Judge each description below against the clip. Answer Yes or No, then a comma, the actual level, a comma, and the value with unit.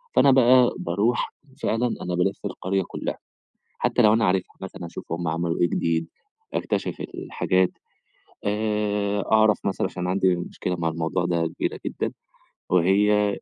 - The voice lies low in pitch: Yes, very low, 95 Hz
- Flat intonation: No, average, 3.2 semitones